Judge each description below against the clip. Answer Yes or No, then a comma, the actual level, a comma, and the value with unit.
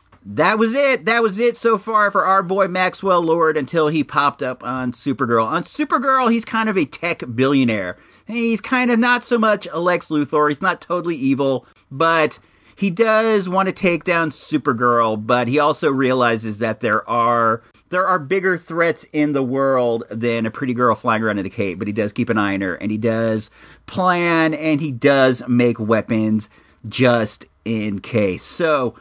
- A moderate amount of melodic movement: No, wide, 8.0 semitones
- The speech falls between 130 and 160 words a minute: No, average, 190 wpm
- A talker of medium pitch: Yes, medium, 145 Hz